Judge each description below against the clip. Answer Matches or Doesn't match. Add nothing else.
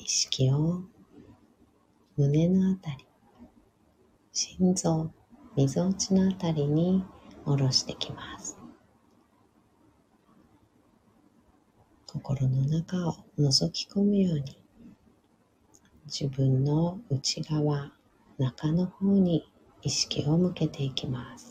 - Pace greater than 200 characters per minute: Doesn't match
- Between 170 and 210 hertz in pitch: Doesn't match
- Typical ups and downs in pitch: Matches